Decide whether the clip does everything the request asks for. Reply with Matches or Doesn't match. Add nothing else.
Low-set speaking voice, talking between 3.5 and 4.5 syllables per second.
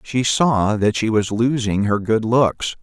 Matches